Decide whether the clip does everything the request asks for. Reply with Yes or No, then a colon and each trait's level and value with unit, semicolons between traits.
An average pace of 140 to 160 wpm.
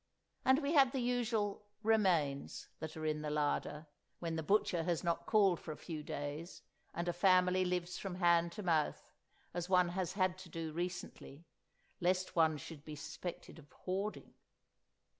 No: average, 170 wpm